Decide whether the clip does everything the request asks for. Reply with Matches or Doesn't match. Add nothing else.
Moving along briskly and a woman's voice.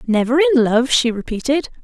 Doesn't match